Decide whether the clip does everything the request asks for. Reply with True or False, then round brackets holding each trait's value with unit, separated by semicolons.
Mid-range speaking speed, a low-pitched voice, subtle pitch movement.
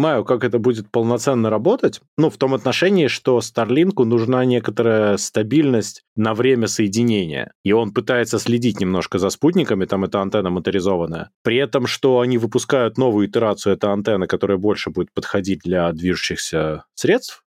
False (150 wpm; 110 Hz; 4.0 semitones)